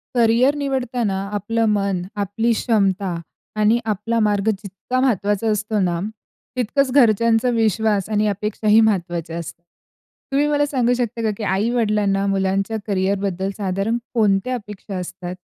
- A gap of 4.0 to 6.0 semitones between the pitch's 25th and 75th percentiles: No, average, 2.9 semitones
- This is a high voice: Yes, high, 210 Hz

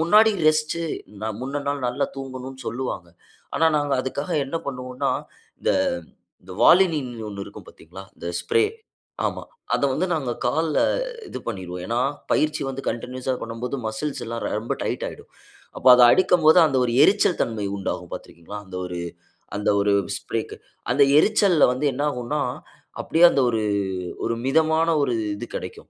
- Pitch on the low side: Yes, low, 130 Hz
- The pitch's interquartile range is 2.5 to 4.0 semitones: No, average, 5.0 semitones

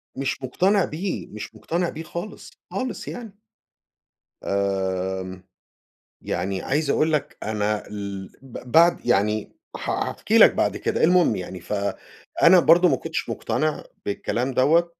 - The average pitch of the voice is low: Yes, low, 130 Hz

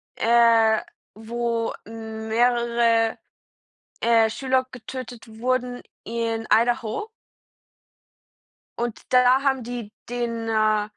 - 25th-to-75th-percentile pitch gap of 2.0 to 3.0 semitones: No, narrow, 1.5 semitones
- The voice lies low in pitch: No, high, 235 Hz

